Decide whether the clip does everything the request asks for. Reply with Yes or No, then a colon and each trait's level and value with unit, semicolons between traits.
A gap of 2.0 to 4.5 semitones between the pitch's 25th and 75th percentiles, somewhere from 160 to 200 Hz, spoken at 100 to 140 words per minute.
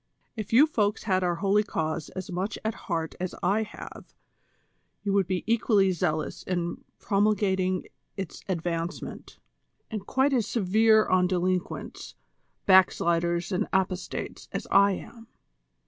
Yes: average, 3.0 semitones; high, 190 Hz; slow, 135 wpm